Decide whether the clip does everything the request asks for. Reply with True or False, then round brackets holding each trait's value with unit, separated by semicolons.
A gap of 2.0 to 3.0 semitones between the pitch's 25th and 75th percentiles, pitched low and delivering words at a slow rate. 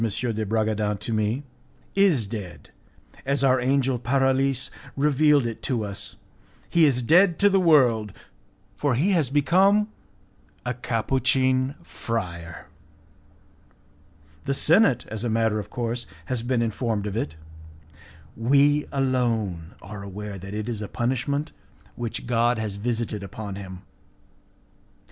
False (4.3 semitones; 120 Hz; 130 wpm)